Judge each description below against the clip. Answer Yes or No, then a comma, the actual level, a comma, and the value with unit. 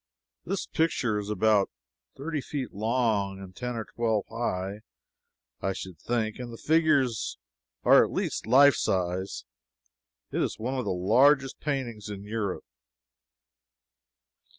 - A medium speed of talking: No, slow, 130 wpm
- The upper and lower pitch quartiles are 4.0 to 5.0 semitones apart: Yes, average, 4.5 semitones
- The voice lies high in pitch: No, low, 115 Hz